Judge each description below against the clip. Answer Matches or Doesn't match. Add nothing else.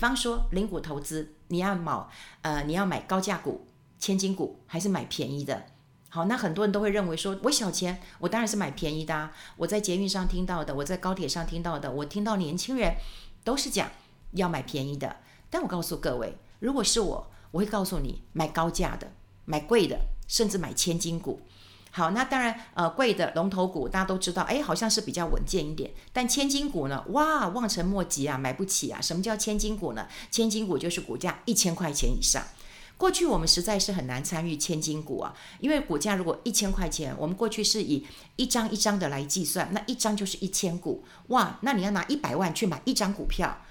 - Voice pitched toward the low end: Doesn't match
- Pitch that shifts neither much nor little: Matches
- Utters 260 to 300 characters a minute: Doesn't match